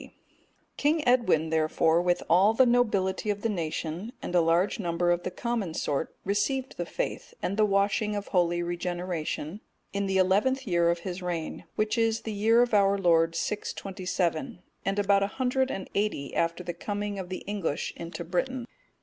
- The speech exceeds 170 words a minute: Yes, average, 180 wpm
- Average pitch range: Yes, average, 3.7 semitones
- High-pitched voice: Yes, high, 195 Hz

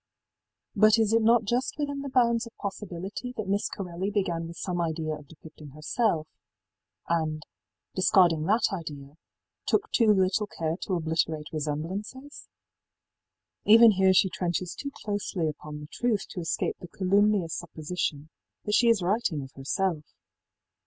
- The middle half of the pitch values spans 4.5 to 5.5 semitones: Yes, average, 5.1 semitones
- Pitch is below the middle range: No, medium, 185 Hz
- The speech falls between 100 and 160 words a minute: Yes, average, 150 wpm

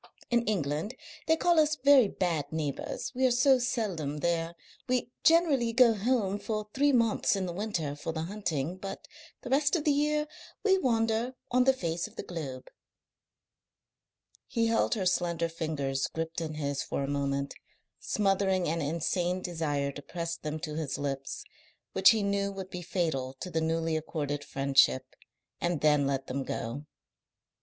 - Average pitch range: No, wide, 7.3 semitones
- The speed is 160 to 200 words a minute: Yes, average, 165 wpm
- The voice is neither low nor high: Yes, medium, 175 Hz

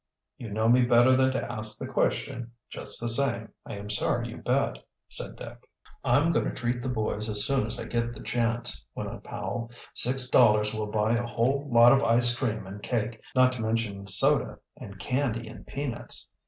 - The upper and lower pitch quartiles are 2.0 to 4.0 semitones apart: Yes, narrow, 2.4 semitones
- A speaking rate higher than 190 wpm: Yes, average, 200 wpm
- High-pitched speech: No, low, 120 Hz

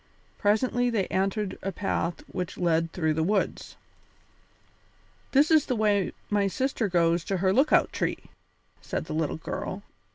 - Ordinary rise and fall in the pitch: Yes, average, 4.0 semitones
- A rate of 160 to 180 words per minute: No, average, 150 wpm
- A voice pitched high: Yes, high, 195 Hz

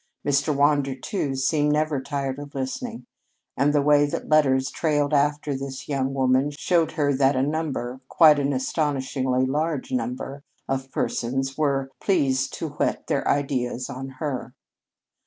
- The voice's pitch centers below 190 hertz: Yes, medium, 140 Hz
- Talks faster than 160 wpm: No, average, 150 wpm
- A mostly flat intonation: Yes, narrow, 1.9 semitones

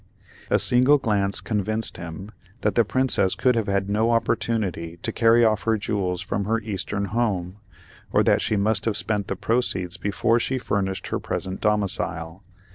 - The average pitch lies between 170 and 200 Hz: No, low, 105 Hz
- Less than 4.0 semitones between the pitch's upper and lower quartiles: Yes, average, 3.0 semitones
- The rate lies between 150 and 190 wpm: Yes, average, 170 wpm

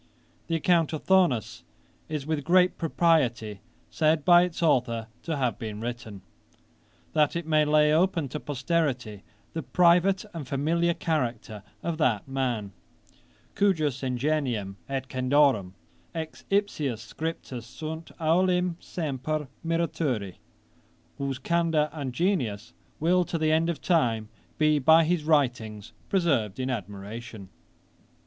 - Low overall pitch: No, medium, 150 Hz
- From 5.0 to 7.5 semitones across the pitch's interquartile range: Yes, wide, 5.5 semitones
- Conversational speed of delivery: No, slow, 125 wpm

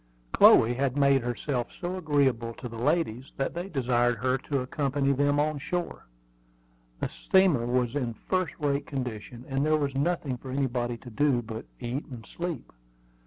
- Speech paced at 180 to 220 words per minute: No, average, 165 wpm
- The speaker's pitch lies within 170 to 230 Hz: No, low, 135 Hz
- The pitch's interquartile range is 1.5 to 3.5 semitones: Yes, average, 3.2 semitones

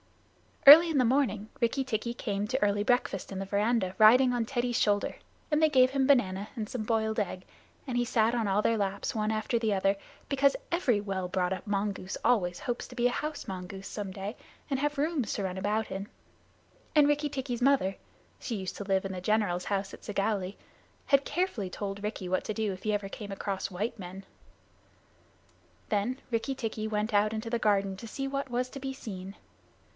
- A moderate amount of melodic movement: Yes, average, 4.2 semitones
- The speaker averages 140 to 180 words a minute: No, average, 200 wpm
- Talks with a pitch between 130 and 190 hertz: No, high, 215 Hz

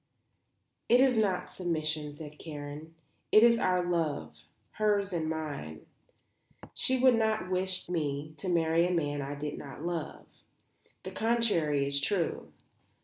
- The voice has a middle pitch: Yes, medium, 165 Hz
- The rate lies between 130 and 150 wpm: Yes, average, 140 wpm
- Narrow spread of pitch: No, average, 4.6 semitones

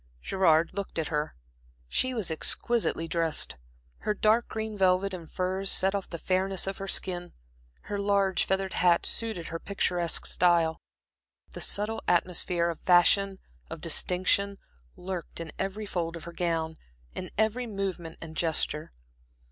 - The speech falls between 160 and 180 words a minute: No, average, 150 wpm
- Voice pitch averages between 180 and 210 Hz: Yes, medium, 185 Hz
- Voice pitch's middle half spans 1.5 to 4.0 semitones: Yes, average, 2.9 semitones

